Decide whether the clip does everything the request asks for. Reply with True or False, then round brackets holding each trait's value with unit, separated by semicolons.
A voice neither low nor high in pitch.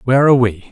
False (125 Hz)